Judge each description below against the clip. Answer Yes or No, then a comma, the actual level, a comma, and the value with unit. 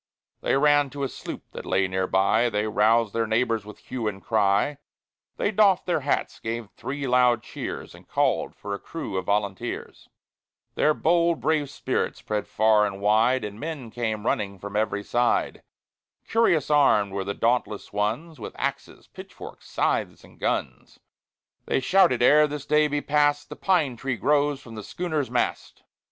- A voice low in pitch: Yes, low, 120 Hz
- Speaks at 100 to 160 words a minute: No, average, 175 wpm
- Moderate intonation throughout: No, wide, 5.8 semitones